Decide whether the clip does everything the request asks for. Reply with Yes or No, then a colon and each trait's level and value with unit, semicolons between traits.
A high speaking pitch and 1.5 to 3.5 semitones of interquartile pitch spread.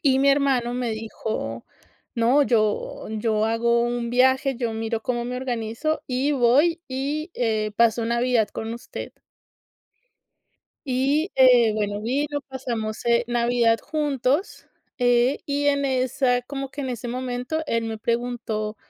Yes: high, 245 Hz; average, 2.7 semitones